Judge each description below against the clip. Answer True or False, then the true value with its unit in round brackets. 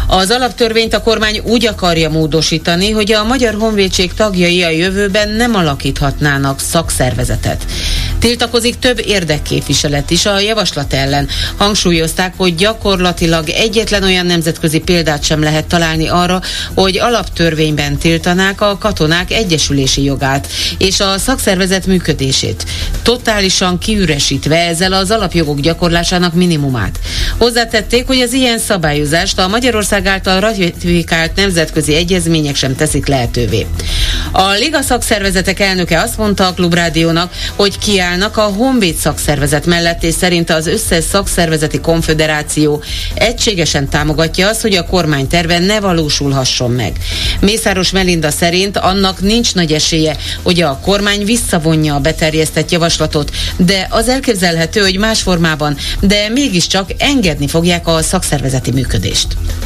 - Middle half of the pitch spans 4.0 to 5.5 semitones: True (5.0 semitones)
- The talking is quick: False (125 wpm)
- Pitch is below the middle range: False (170 Hz)